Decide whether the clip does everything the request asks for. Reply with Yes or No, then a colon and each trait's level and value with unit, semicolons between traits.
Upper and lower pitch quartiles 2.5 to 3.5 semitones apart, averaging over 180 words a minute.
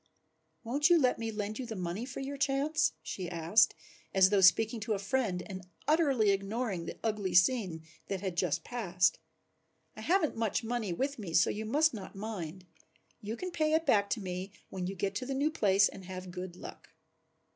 No: wide, 5.4 semitones; average, 200 wpm